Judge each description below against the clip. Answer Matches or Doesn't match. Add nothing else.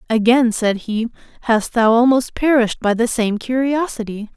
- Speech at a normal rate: Matches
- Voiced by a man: Doesn't match